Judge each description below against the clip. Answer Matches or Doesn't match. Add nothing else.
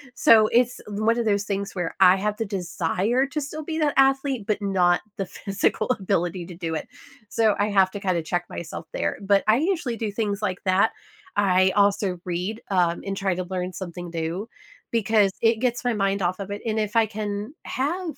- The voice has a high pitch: Matches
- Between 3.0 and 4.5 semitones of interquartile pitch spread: Matches